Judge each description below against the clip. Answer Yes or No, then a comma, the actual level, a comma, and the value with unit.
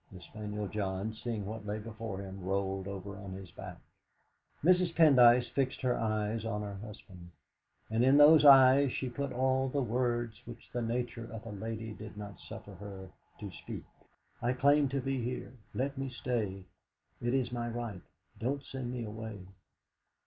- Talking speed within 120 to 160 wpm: No, average, 170 wpm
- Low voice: Yes, low, 115 Hz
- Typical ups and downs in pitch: Yes, average, 3.9 semitones